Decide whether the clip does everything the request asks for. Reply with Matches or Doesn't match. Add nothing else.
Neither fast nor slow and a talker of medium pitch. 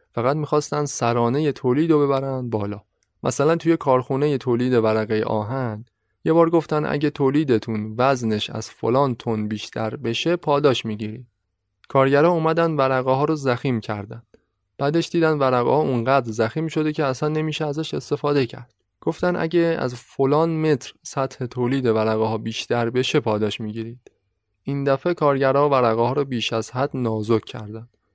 Doesn't match